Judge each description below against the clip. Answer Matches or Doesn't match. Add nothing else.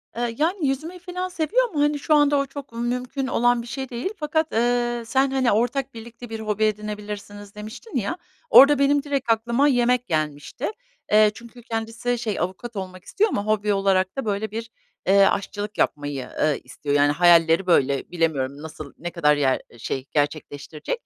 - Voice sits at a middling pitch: Doesn't match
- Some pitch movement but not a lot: Doesn't match